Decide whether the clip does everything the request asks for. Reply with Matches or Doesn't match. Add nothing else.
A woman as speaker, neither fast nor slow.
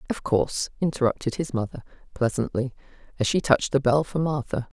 Matches